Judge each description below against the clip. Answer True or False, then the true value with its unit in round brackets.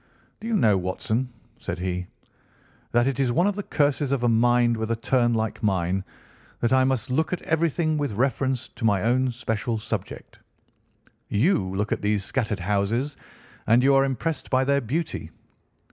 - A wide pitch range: False (4.3 semitones)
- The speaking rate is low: False (175 wpm)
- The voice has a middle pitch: False (120 Hz)